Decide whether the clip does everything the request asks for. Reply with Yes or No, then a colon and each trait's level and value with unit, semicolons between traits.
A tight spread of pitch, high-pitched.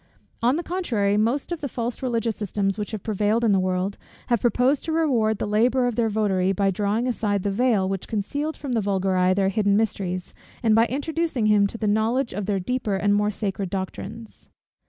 No: average, 3.5 semitones; high, 215 Hz